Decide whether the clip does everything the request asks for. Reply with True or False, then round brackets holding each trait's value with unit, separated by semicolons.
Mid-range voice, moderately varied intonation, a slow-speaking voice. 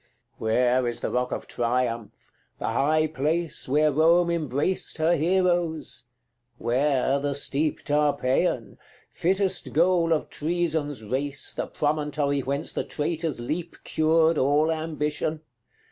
True (150 Hz; 3.2 semitones; 125 wpm)